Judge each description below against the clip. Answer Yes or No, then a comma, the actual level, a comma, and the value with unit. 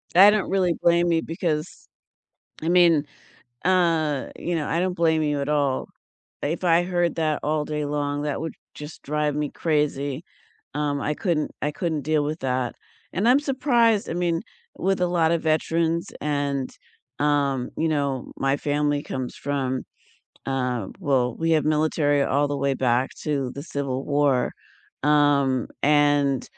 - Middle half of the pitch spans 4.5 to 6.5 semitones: No, average, 2.9 semitones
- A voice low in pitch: No, medium, 150 Hz